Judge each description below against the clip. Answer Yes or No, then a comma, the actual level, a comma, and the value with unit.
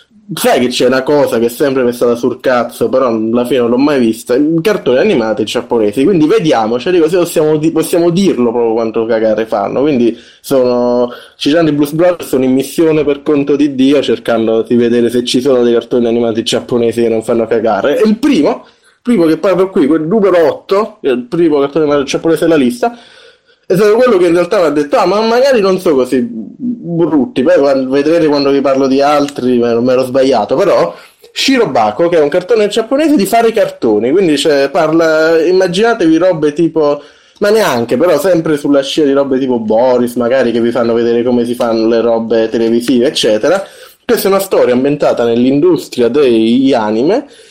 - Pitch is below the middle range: No, medium, 145 Hz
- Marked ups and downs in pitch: Yes, wide, 7.2 semitones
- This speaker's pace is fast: Yes, fast, 195 wpm